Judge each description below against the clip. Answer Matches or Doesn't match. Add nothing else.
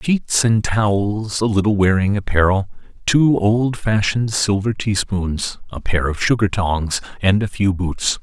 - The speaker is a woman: Doesn't match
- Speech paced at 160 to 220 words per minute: Doesn't match